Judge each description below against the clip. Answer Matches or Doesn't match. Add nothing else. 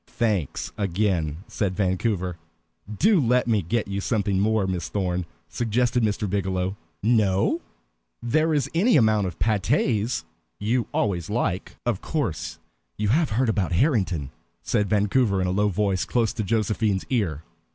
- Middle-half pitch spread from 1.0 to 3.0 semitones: Doesn't match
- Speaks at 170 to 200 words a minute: Doesn't match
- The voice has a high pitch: Doesn't match